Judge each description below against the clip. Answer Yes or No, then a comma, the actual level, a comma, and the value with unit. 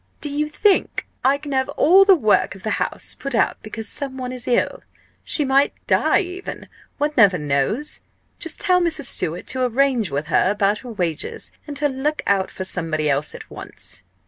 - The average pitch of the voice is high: Yes, very high, 255 Hz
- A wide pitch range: Yes, wide, 7.0 semitones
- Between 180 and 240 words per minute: Yes, average, 195 wpm